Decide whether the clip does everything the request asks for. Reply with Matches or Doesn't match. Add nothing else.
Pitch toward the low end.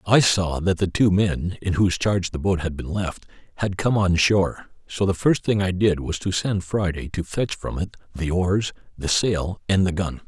Matches